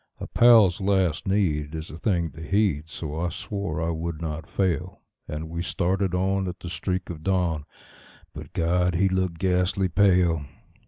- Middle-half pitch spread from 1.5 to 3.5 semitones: Yes, average, 2.8 semitones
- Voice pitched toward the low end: Yes, very low, 90 Hz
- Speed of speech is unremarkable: Yes, average, 170 wpm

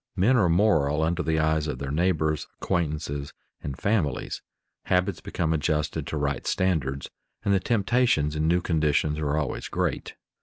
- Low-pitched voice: Yes, very low, 80 Hz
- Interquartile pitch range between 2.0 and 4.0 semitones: Yes, average, 3.6 semitones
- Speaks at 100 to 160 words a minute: Yes, average, 155 wpm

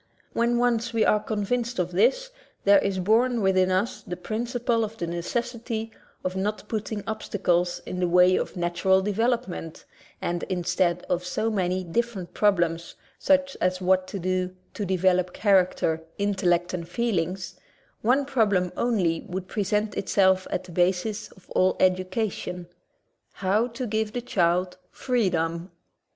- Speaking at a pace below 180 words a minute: Yes, average, 150 wpm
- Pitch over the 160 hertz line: Yes, high, 190 Hz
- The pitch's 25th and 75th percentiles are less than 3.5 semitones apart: No, average, 3.8 semitones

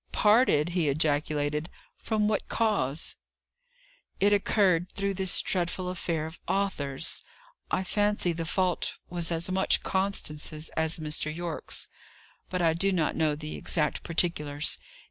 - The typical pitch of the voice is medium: Yes, medium, 170 Hz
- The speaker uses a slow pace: Yes, slow, 130 wpm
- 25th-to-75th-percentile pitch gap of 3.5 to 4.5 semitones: Yes, average, 3.8 semitones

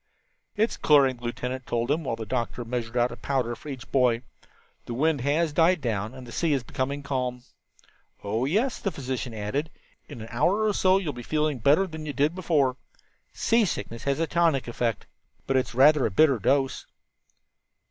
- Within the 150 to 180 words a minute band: No, average, 195 wpm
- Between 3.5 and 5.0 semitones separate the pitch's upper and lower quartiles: Yes, average, 4.3 semitones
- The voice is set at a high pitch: No, low, 135 Hz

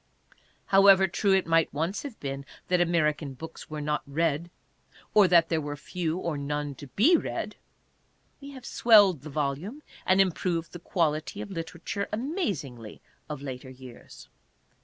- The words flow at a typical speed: Yes, average, 155 wpm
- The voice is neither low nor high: Yes, medium, 165 Hz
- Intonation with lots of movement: No, average, 4.8 semitones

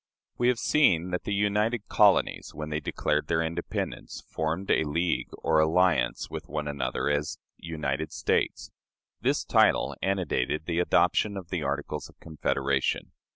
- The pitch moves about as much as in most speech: Yes, average, 3.7 semitones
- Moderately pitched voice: No, very low, 80 Hz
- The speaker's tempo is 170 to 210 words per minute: No, average, 150 wpm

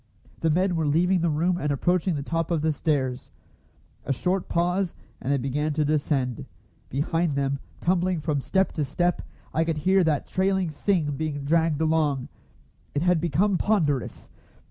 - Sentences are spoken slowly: No, average, 165 wpm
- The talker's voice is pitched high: No, medium, 160 Hz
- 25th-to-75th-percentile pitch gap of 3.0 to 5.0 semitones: Yes, average, 3.5 semitones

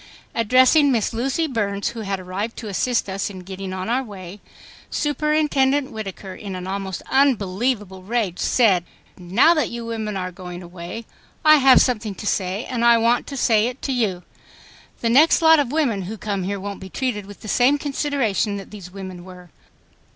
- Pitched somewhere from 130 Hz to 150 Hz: No, high, 215 Hz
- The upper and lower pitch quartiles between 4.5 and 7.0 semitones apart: Yes, average, 5.1 semitones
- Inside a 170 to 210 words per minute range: Yes, average, 185 wpm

